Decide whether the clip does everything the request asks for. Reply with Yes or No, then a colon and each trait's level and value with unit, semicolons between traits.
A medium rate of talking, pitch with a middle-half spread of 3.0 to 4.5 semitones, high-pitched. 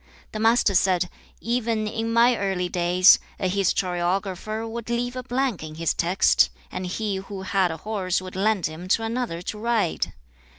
Yes: average, 170 wpm; average, 3.9 semitones; high, 195 Hz